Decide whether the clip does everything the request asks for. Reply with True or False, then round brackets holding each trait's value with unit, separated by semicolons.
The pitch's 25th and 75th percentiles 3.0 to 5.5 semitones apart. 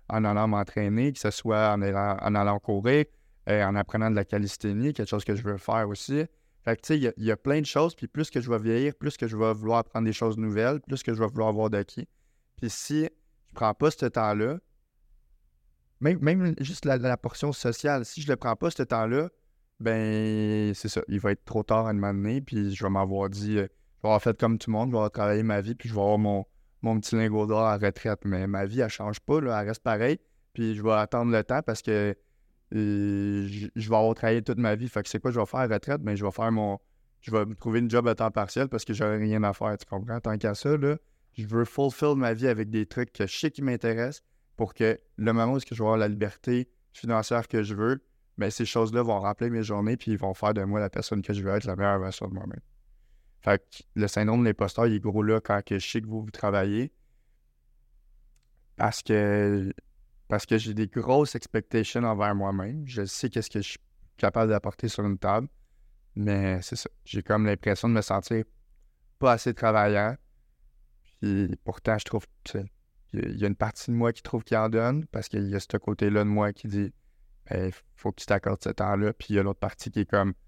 False (2.5 semitones)